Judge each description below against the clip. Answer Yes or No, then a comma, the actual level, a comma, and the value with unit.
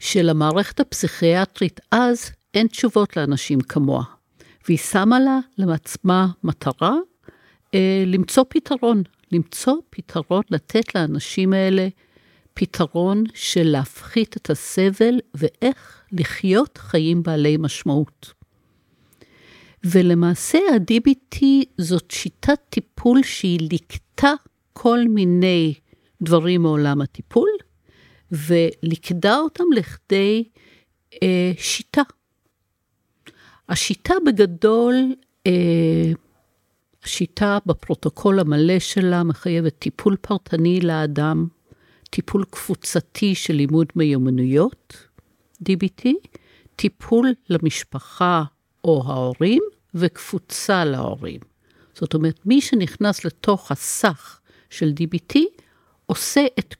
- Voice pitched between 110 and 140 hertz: No, medium, 185 Hz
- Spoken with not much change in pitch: No, wide, 5.6 semitones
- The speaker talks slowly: Yes, slow, 85 wpm